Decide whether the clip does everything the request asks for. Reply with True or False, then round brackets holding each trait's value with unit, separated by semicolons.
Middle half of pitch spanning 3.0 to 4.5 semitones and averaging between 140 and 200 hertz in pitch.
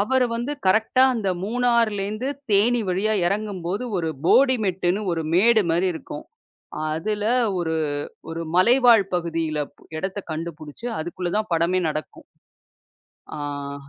False (5.0 semitones; 190 Hz)